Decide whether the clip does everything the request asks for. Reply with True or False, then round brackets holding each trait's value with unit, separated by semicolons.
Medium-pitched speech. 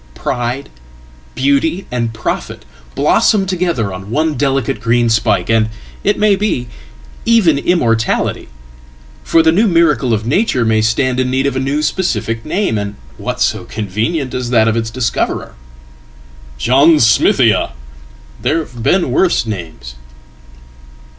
False (125 Hz)